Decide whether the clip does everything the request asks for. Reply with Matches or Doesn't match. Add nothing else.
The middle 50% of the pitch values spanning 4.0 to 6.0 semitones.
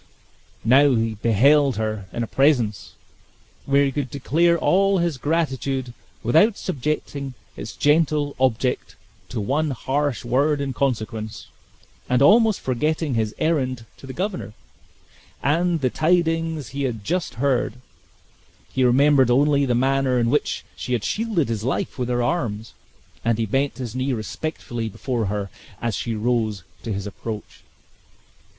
Matches